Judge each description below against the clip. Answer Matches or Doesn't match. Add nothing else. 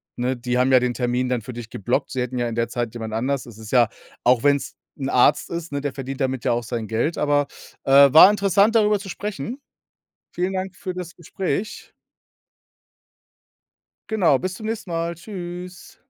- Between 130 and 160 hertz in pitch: Matches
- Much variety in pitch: Matches